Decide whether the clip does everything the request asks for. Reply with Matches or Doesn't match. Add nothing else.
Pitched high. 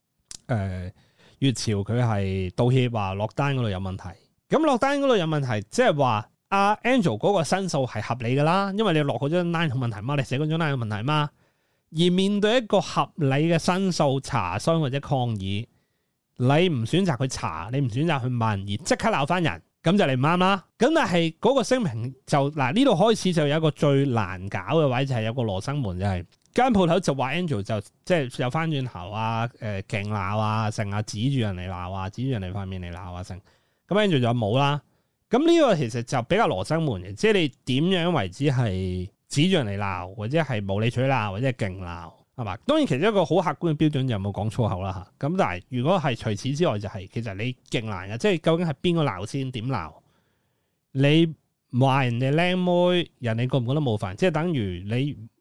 Doesn't match